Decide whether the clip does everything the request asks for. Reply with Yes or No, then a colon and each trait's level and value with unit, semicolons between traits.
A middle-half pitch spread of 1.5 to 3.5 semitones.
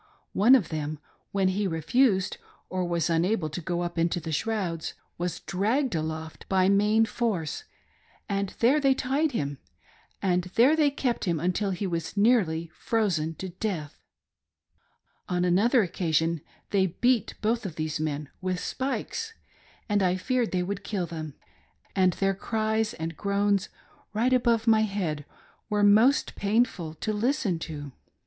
No: average, 5.0 semitones